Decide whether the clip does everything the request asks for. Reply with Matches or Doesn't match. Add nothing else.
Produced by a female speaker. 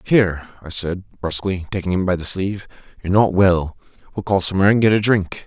Doesn't match